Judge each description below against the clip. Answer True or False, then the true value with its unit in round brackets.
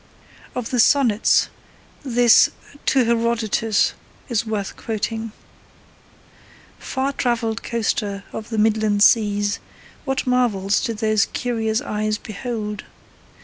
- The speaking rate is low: True (105 wpm)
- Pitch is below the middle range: False (225 Hz)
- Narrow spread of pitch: True (2.1 semitones)